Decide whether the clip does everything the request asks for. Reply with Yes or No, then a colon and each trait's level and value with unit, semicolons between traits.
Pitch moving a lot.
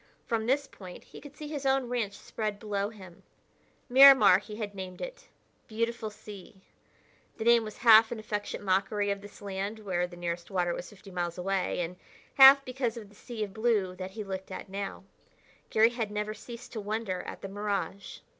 No: average, 3.2 semitones